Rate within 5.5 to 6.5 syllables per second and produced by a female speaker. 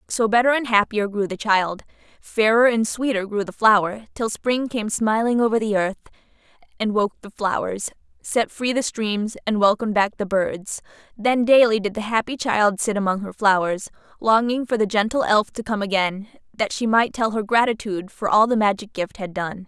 No: 5.1 syllables/s; female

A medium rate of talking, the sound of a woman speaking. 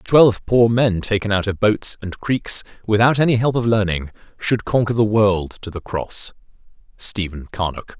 No: average, 175 wpm; male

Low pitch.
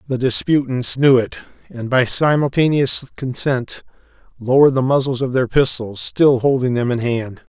Yes: low, 130 Hz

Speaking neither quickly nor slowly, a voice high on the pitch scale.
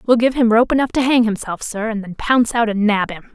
No: fast, 285 wpm; high, 225 Hz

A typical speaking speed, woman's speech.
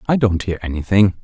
No: average, 195 wpm; male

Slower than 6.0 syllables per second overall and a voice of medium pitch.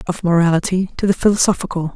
No: 6.8 syllables/s; medium, 180 Hz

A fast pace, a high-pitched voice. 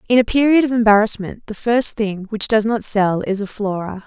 Yes: fast, 220 wpm; high, 215 Hz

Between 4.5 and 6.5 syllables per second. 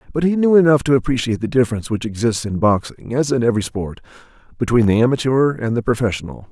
No: 6.9 syllables/s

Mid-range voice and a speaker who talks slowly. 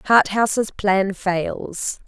No: high, 200 Hz; slow, 85 wpm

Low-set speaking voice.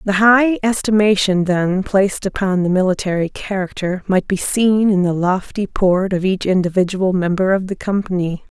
No: high, 190 Hz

